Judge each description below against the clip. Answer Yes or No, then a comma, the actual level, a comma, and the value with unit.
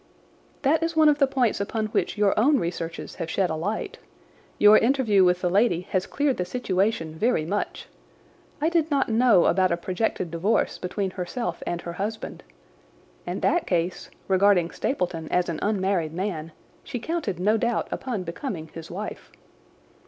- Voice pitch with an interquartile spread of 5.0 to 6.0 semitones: Yes, wide, 5.4 semitones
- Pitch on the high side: Yes, high, 195 Hz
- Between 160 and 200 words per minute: Yes, average, 165 wpm